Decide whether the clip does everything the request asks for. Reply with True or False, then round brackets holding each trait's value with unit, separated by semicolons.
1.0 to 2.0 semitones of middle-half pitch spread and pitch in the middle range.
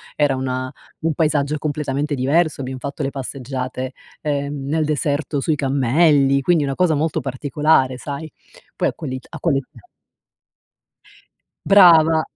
False (2.6 semitones; 145 Hz)